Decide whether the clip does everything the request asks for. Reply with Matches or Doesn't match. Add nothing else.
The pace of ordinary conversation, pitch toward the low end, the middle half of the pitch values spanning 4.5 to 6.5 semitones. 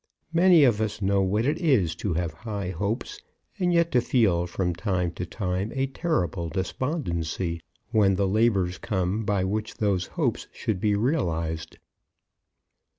Matches